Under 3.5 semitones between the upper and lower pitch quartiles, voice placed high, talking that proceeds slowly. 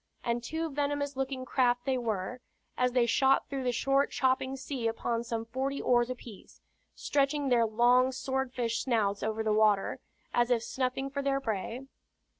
No: narrow, 2.6 semitones; very high, 250 Hz; average, 170 wpm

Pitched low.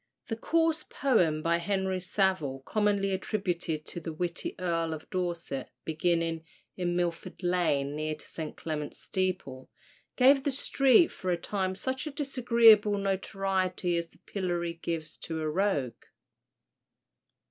No: medium, 180 Hz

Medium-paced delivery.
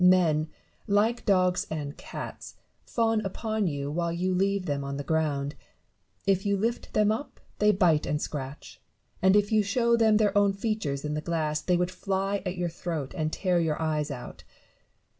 Yes: average, 180 wpm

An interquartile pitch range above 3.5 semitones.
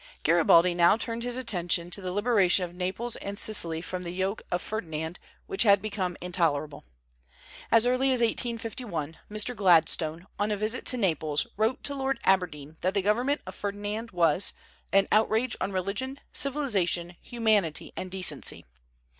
Yes: average, 4.6 semitones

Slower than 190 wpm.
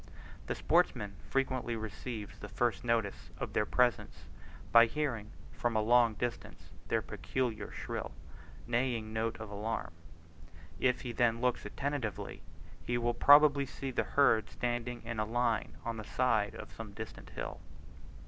Yes: average, 150 wpm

